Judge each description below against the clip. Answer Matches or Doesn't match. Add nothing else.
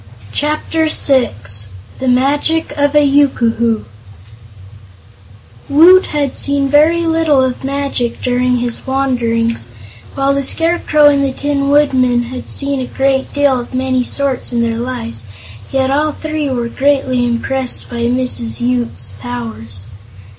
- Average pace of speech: Doesn't match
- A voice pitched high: Matches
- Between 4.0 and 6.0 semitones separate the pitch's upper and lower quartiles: Doesn't match